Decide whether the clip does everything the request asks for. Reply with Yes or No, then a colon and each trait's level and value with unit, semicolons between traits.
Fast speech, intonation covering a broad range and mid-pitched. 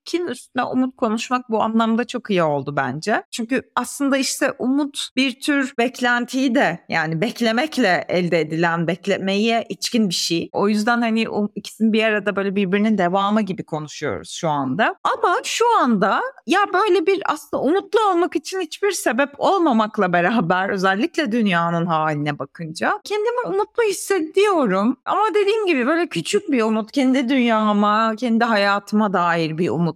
No: fast, 145 wpm; wide, 6.9 semitones; high, 235 Hz